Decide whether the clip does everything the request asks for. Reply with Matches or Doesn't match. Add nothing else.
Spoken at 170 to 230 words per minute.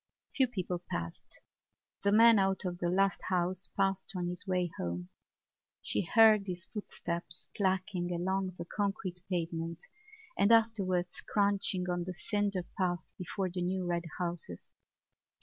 Doesn't match